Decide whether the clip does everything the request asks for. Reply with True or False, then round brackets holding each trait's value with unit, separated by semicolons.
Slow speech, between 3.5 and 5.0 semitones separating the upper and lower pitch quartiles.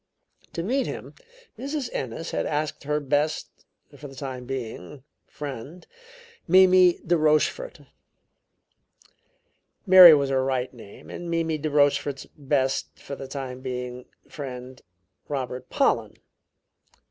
True (120 wpm; 3.9 semitones)